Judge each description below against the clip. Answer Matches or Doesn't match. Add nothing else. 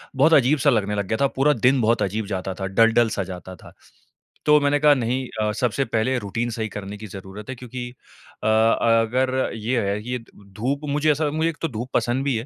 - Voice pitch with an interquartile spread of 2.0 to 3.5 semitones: Doesn't match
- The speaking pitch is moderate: Doesn't match